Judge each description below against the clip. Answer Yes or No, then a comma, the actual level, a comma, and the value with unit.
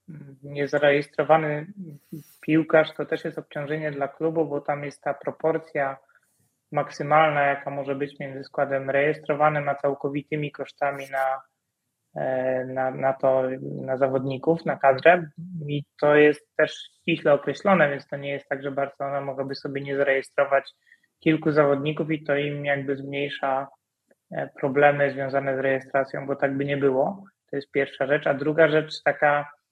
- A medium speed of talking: Yes, average, 145 wpm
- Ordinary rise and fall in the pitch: No, narrow, 1.8 semitones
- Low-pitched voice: No, medium, 145 Hz